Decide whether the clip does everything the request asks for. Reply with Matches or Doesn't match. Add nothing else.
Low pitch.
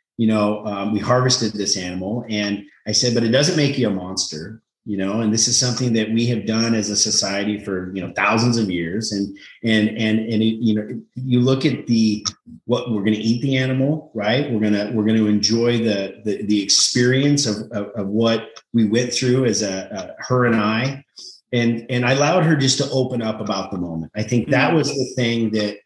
Matches